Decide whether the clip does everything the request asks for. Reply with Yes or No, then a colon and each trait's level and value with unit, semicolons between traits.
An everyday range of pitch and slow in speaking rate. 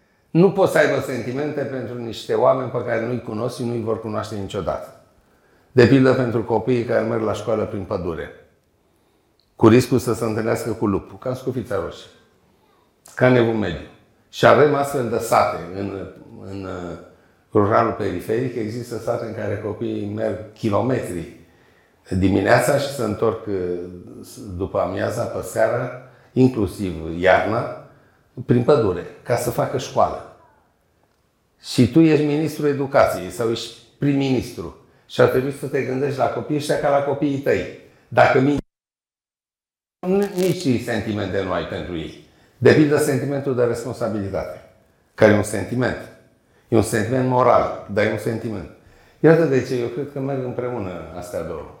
No: average, 3.7 semitones; average, 150 wpm